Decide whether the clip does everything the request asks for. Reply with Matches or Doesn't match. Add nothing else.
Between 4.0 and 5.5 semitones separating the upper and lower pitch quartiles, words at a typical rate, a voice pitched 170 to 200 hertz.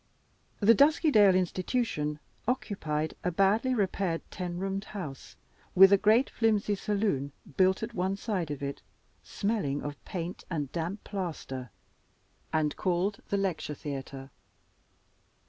Doesn't match